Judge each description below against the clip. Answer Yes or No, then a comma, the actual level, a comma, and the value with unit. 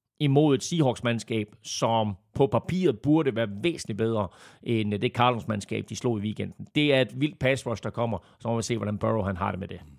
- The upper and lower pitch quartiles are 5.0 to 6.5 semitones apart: No, average, 3.4 semitones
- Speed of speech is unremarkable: Yes, average, 210 wpm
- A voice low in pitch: Yes, low, 115 Hz